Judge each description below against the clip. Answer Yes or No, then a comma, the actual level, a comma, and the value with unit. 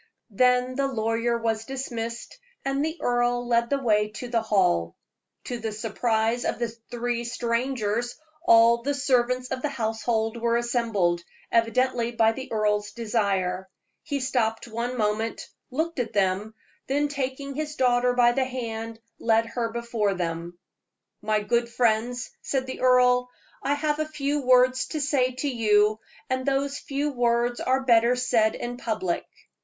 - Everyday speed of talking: Yes, average, 155 wpm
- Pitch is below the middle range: No, high, 240 Hz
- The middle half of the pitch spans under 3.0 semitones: Yes, narrow, 2.5 semitones